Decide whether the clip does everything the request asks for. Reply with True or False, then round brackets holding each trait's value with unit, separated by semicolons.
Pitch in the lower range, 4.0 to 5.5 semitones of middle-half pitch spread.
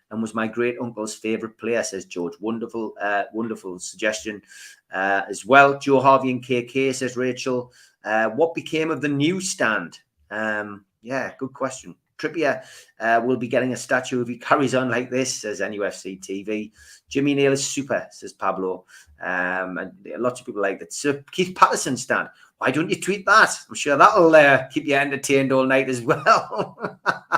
True (125 Hz; 4.3 semitones)